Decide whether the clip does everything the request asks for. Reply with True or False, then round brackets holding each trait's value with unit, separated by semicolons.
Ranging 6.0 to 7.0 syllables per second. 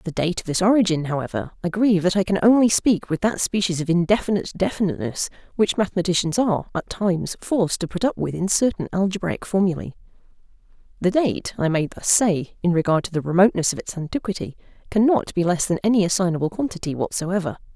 True (6.4 syllables/s)